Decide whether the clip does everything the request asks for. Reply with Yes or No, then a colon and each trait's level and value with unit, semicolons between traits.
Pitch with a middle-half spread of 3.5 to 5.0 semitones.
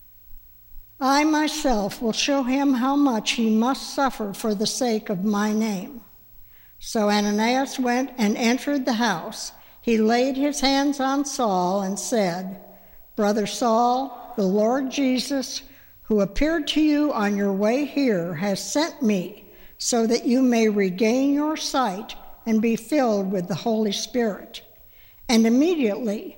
Yes: average, 4.5 semitones